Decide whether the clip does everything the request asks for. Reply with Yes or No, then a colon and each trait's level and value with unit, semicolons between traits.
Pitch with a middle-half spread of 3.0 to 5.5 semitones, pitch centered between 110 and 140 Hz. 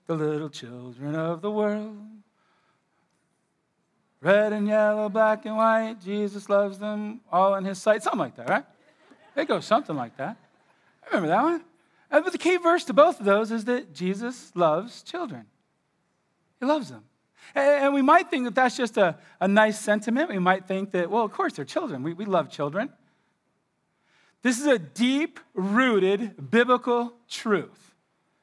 No: average, 4.6 semitones; high, 215 Hz